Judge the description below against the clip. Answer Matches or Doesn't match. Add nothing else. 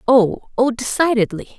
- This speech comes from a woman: Matches